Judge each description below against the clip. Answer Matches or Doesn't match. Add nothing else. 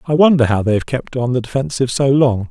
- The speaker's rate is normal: Doesn't match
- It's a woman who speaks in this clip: Doesn't match